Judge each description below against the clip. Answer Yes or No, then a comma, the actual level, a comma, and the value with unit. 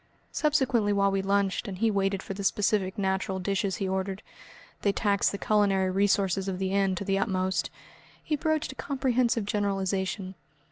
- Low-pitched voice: No, high, 195 Hz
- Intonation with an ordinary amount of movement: No, narrow, 1.6 semitones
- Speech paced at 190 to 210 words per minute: No, average, 170 wpm